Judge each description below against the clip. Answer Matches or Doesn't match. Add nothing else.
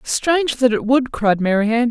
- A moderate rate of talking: Matches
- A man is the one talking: Doesn't match